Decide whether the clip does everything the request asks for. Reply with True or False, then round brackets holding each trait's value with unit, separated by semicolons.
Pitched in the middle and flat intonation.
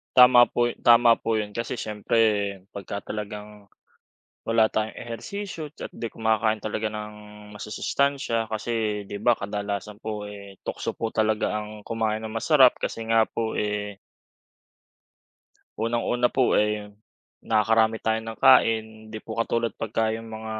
False (110 Hz; 1.6 semitones)